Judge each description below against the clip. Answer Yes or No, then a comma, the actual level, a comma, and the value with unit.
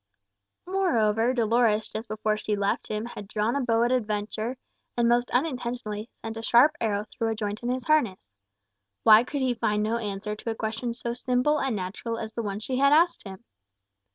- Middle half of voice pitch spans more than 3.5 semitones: No, average, 2.7 semitones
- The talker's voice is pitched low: No, high, 225 Hz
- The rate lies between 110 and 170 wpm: No, average, 200 wpm